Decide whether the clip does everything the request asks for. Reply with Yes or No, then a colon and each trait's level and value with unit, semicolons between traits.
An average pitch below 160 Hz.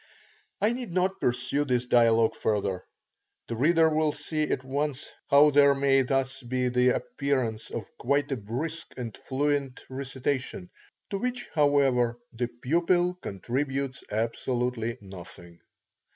Yes: low, 135 Hz